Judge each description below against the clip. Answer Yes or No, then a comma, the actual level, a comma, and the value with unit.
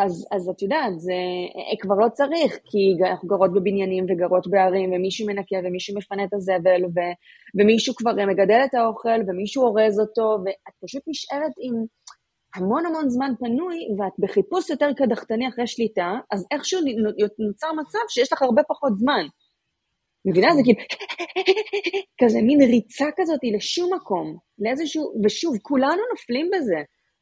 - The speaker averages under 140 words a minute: No, average, 145 wpm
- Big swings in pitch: Yes, wide, 6.6 semitones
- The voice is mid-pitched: No, high, 225 Hz